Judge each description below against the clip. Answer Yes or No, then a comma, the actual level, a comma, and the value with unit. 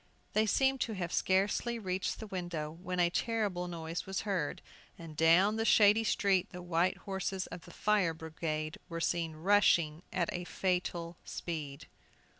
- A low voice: No, medium, 180 Hz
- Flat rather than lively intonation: No, average, 3.2 semitones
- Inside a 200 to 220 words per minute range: No, average, 160 wpm